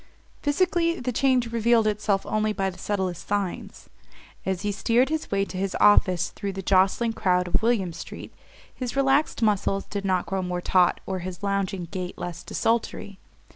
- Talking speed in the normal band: Yes, average, 175 wpm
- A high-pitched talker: Yes, high, 200 Hz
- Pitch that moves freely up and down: No, average, 3.9 semitones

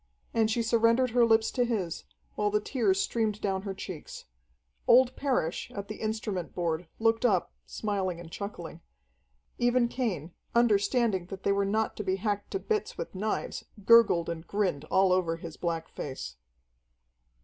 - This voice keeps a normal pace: Yes, average, 160 wpm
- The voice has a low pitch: No, high, 205 Hz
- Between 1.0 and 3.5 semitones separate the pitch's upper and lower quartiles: No, average, 4.2 semitones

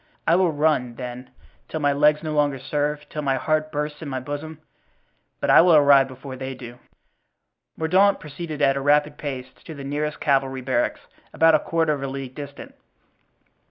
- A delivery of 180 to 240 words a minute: Yes, average, 185 wpm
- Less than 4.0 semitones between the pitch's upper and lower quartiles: Yes, narrow, 2.4 semitones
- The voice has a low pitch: No, medium, 145 Hz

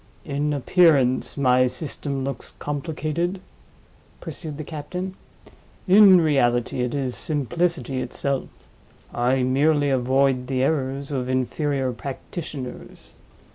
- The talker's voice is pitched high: No, medium, 140 Hz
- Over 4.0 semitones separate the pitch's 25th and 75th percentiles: No, average, 3.1 semitones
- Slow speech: Yes, slow, 100 wpm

